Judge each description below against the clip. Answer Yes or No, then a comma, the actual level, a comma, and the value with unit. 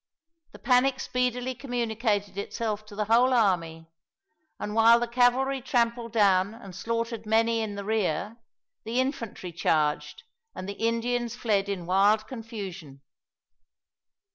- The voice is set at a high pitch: Yes, high, 225 Hz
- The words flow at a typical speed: No, slow, 130 wpm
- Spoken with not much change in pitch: No, average, 3.1 semitones